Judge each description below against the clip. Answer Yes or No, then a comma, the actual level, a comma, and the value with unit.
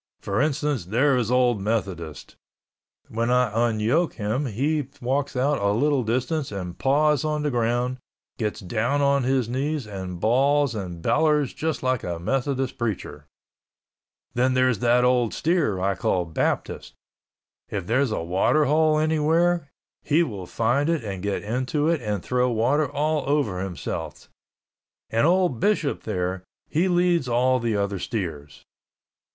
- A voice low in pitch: Yes, low, 125 Hz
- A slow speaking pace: No, average, 145 wpm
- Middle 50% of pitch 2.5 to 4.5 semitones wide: No, wide, 5.5 semitones